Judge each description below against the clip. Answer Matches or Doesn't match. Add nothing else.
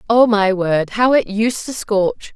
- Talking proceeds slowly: Doesn't match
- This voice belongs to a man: Doesn't match